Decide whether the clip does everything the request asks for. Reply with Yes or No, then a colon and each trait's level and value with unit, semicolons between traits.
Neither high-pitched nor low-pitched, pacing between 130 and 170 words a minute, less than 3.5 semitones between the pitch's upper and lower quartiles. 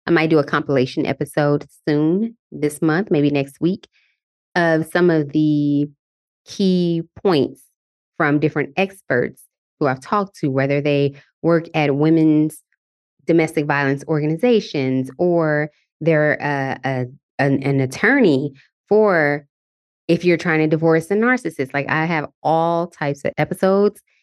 Yes: medium, 155 Hz; slow, 135 wpm; average, 2.9 semitones